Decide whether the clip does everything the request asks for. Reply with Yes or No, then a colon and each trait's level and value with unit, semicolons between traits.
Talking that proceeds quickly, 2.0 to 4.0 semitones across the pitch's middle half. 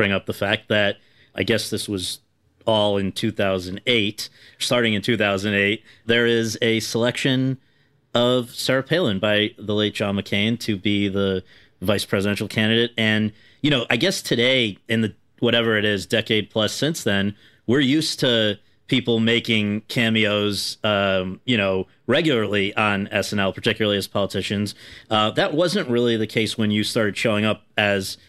No: average, 160 wpm; narrow, 2.5 semitones